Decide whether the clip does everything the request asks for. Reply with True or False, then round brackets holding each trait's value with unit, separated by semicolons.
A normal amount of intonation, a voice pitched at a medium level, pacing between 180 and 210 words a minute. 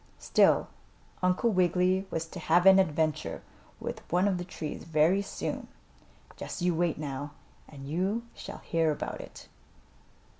False (3.1 semitones; 175 Hz; 145 wpm)